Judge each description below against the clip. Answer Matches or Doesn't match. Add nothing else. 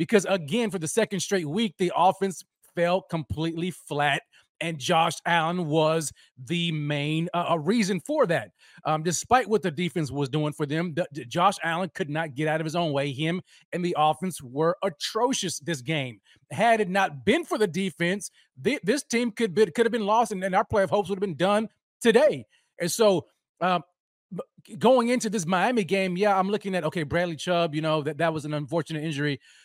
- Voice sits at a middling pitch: Matches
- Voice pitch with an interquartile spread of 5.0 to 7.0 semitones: Doesn't match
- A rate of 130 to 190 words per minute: Doesn't match